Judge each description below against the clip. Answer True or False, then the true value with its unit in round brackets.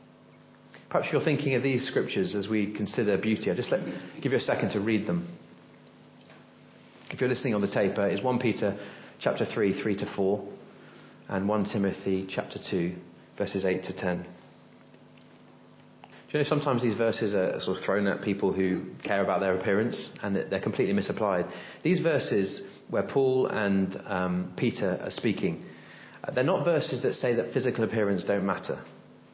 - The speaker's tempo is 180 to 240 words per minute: False (170 wpm)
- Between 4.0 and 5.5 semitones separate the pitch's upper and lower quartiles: False (2.9 semitones)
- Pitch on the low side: True (100 Hz)